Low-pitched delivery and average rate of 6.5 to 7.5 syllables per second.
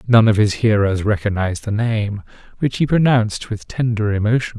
No: low, 110 Hz; 5.4 syllables/s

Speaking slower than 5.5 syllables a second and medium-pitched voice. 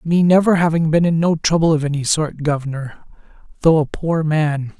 Yes: 5.0 syllables/s; medium, 155 Hz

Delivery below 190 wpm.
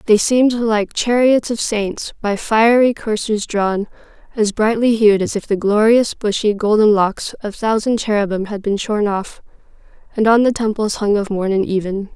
Yes: average, 180 wpm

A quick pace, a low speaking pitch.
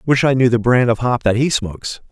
Yes: fast, 285 wpm; low, 120 Hz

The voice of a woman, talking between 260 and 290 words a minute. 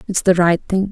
Yes: female; fast, 265 wpm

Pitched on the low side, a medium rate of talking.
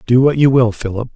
No: low, 125 Hz; fast, 260 wpm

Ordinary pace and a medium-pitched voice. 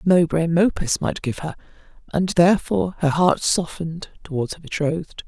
Yes: average, 160 wpm; medium, 165 Hz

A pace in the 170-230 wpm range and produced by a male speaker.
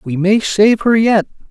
Yes: average, 200 wpm; male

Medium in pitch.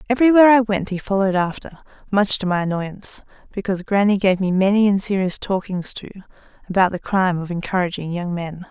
No: high, 195 Hz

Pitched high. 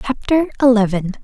Yes: high, 235 Hz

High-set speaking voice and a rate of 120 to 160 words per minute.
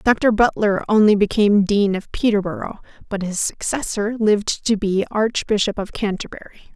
Yes: high, 205 Hz; average, 140 wpm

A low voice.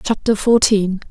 No: high, 210 Hz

